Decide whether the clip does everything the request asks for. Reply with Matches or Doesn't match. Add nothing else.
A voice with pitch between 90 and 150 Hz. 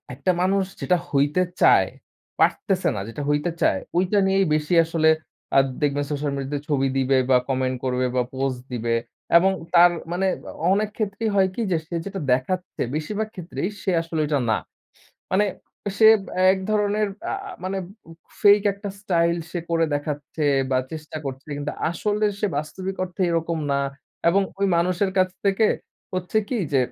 Doesn't match